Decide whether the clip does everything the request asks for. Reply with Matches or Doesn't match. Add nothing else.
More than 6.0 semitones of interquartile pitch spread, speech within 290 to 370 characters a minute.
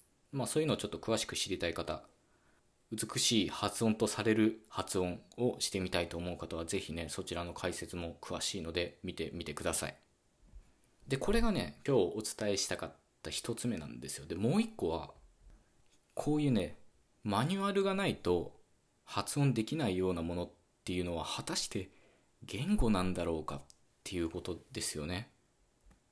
Doesn't match